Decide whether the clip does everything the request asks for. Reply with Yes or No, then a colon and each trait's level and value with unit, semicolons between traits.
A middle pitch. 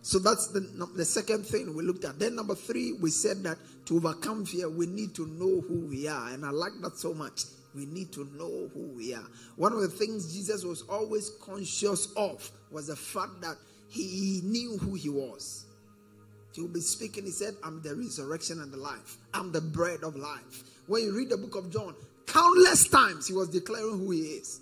Yes: medium, 180 Hz